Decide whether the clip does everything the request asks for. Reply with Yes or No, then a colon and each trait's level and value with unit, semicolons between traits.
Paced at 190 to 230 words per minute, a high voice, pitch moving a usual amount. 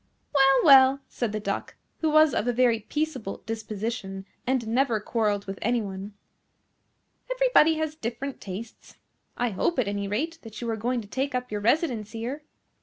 No: average, 175 wpm; high, 235 Hz; average, 4.5 semitones